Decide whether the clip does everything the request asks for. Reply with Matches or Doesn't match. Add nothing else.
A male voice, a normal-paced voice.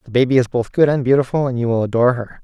Doesn't match